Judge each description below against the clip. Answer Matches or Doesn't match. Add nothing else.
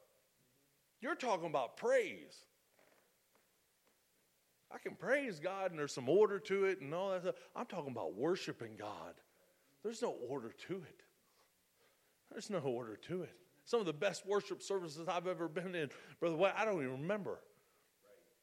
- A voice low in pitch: Doesn't match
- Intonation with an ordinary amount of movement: Matches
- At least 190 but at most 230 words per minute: Doesn't match